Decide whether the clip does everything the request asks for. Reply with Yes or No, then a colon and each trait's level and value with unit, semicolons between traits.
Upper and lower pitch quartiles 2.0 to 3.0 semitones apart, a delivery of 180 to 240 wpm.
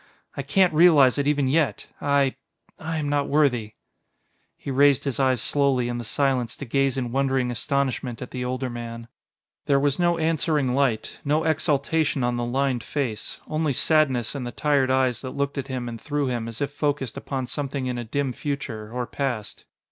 Yes: average, 2.7 semitones; average, 190 wpm